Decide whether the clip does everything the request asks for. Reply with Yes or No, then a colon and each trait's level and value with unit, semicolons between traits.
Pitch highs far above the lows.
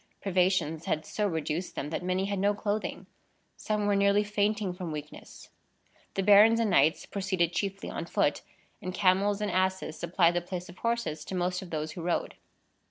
No: average, 2.8 semitones